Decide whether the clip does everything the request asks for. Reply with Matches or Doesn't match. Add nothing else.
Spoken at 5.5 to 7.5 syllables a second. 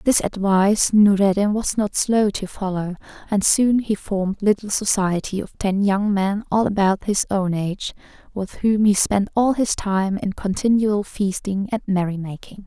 Doesn't match